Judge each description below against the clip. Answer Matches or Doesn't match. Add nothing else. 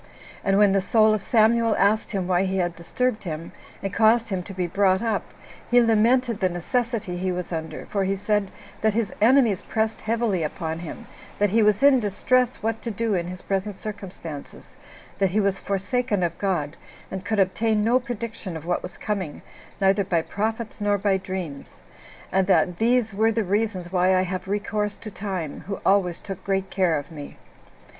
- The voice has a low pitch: Doesn't match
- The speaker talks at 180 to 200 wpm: Matches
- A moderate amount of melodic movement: Matches